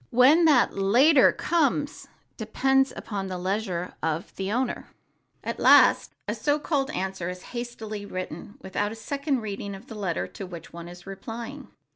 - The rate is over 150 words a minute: Yes, average, 160 wpm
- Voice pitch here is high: Yes, high, 215 Hz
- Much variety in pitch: Yes, wide, 6.0 semitones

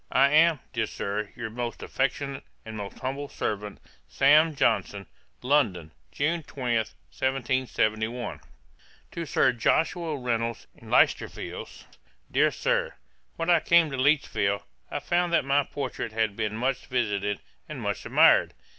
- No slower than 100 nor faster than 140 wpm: Yes, slow, 135 wpm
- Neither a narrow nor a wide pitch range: Yes, average, 4.7 semitones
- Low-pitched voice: Yes, low, 130 Hz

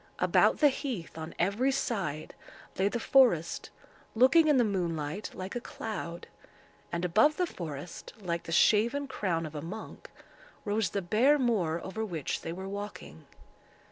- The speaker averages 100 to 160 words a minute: Yes, average, 155 wpm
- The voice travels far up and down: Yes, wide, 6.0 semitones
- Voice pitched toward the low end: No, high, 200 Hz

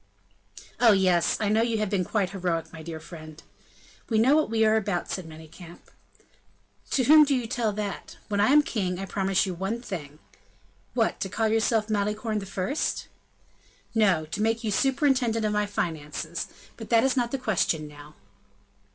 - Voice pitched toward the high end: Yes, high, 210 Hz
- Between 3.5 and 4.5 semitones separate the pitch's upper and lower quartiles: Yes, average, 4.1 semitones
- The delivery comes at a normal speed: Yes, average, 180 wpm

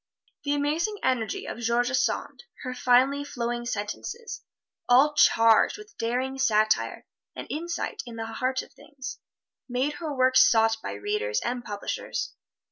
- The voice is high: Yes, very high, 255 Hz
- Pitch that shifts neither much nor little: Yes, average, 3.8 semitones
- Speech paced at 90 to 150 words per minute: Yes, average, 140 wpm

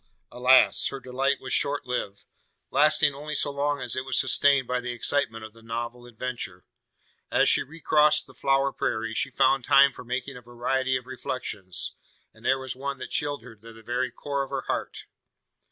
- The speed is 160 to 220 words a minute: Yes, average, 190 wpm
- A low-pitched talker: Yes, low, 130 Hz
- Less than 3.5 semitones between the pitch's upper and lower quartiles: Yes, narrow, 2.5 semitones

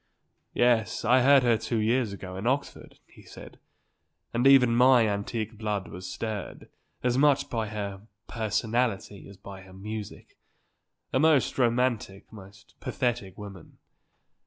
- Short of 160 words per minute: Yes, slow, 135 wpm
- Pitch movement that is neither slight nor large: Yes, average, 3.7 semitones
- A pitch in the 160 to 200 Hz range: No, low, 110 Hz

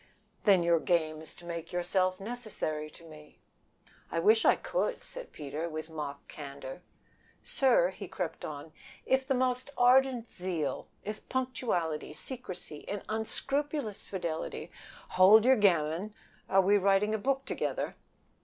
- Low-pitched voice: No, high, 190 Hz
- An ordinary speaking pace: Yes, average, 145 wpm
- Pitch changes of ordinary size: No, wide, 6.9 semitones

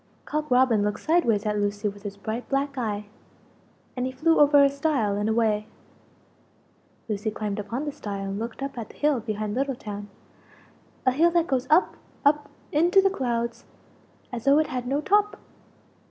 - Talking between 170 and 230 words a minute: Yes, average, 180 wpm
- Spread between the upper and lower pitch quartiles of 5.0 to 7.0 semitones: Yes, wide, 5.5 semitones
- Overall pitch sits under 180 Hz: No, high, 245 Hz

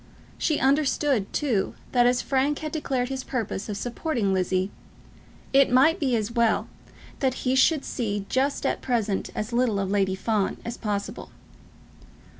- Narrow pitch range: No, average, 4.7 semitones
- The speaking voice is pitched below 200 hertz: No, high, 245 Hz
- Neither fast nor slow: Yes, average, 155 wpm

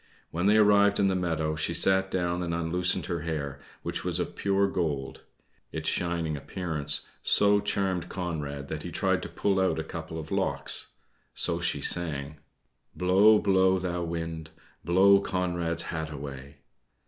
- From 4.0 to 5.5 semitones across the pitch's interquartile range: No, average, 3.2 semitones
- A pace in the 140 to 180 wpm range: Yes, average, 160 wpm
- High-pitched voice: No, very low, 85 Hz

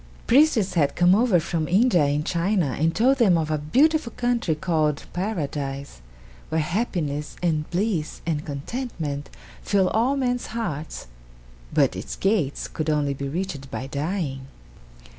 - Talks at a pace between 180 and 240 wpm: No, average, 140 wpm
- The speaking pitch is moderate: Yes, medium, 170 Hz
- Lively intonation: Yes, wide, 6.5 semitones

